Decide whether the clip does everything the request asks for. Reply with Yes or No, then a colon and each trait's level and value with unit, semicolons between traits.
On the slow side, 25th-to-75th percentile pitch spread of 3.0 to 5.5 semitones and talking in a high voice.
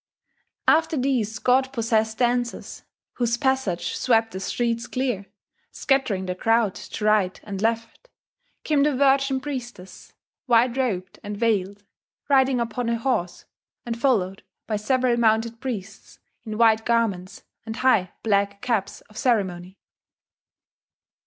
Yes: slow, 125 wpm; average, 3.9 semitones; high, 230 Hz